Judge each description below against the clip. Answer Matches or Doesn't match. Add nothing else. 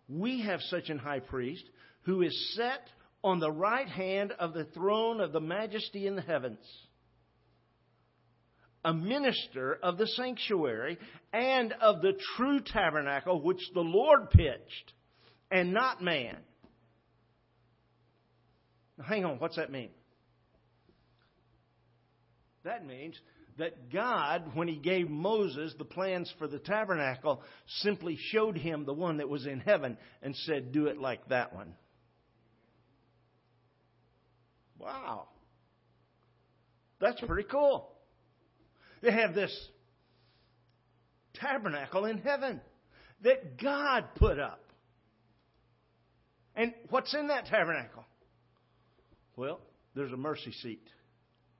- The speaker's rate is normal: Doesn't match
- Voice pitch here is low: Doesn't match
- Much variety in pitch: Matches